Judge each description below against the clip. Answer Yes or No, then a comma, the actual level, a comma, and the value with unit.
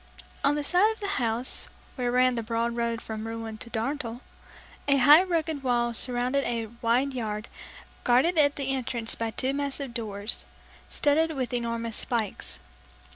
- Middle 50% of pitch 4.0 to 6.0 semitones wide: No, average, 3.4 semitones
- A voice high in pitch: Yes, high, 245 Hz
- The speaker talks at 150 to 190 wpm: Yes, average, 160 wpm